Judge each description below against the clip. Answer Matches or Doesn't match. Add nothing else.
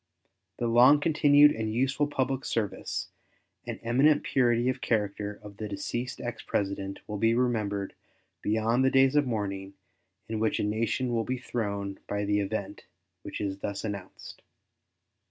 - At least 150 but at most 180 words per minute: Matches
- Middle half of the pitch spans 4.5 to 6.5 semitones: Doesn't match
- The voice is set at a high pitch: Doesn't match